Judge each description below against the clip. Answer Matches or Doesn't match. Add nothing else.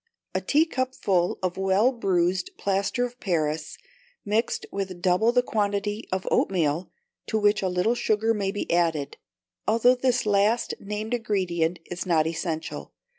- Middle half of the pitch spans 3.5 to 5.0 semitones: Matches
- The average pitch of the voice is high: Matches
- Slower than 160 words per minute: Matches